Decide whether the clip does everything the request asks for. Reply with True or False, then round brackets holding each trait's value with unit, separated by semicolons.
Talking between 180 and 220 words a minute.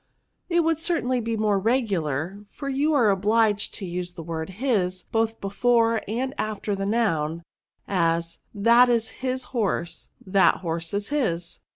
False (160 wpm)